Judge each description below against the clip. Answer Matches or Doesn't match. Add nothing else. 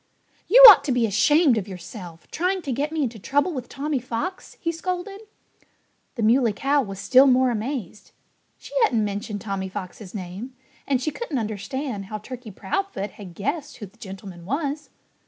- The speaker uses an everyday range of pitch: Doesn't match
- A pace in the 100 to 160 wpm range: Doesn't match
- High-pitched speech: Matches